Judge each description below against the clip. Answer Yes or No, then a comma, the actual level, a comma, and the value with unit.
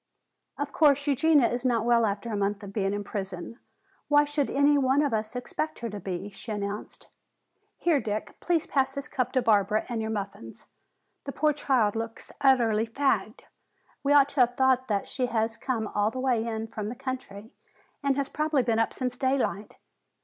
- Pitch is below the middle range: No, high, 240 Hz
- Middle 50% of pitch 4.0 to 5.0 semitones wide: Yes, average, 4.4 semitones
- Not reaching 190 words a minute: No, average, 195 wpm